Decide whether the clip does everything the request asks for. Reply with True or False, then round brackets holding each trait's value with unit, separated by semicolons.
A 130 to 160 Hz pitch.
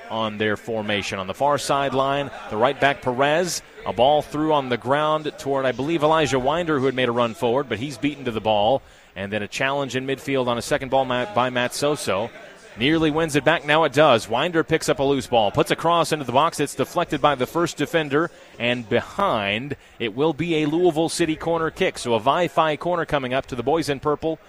True (140 Hz)